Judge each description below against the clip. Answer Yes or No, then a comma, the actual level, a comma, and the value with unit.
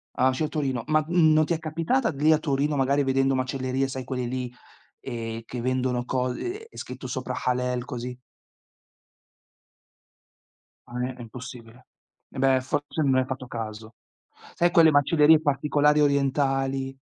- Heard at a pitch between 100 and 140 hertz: Yes, low, 135 Hz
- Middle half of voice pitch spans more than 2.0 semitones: Yes, average, 2.8 semitones